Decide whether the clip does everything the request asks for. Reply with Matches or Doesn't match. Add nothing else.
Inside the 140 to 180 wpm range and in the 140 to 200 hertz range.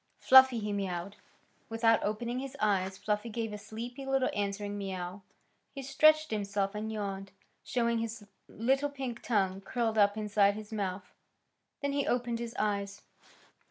Doesn't match